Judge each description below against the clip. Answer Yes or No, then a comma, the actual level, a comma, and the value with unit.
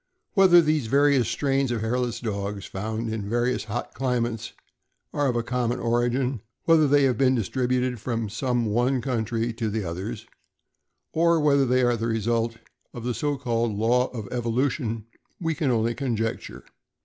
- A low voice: Yes, low, 120 Hz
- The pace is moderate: Yes, average, 165 wpm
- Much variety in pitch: No, average, 2.8 semitones